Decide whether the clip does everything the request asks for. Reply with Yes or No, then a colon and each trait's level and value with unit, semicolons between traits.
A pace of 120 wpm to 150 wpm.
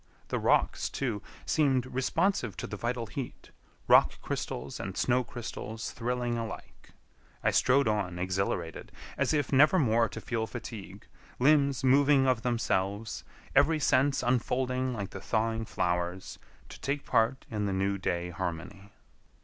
Yes: average, 140 wpm